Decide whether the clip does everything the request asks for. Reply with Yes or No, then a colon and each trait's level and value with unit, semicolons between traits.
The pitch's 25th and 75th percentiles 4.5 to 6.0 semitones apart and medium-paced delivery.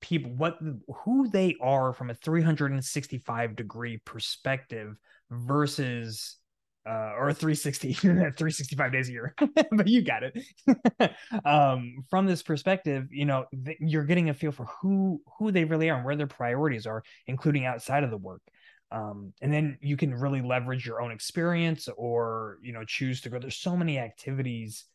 Yes: average, 4.9 semitones; average, 170 wpm